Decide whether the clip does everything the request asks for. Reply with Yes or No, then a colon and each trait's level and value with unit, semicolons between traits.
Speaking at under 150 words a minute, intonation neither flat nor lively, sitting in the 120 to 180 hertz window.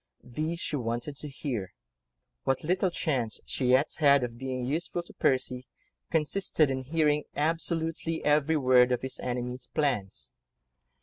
Yes: average, 140 wpm; average, 3.8 semitones; medium, 140 Hz